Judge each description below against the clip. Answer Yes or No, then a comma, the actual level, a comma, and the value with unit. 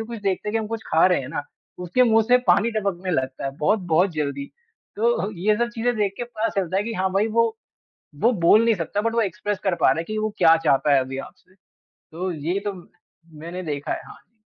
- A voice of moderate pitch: No, high, 195 Hz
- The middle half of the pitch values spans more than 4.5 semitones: Yes, average, 5.2 semitones